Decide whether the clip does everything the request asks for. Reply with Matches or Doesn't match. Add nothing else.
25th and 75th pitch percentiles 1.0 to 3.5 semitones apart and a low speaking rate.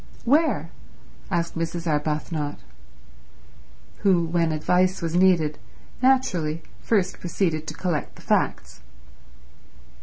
Matches